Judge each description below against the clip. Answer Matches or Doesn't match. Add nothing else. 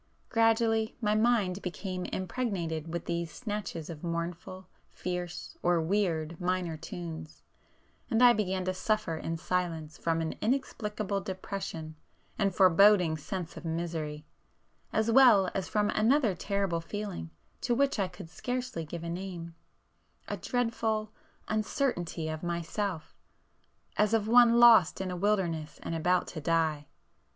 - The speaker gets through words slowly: Matches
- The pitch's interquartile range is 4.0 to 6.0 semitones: Matches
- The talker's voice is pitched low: Doesn't match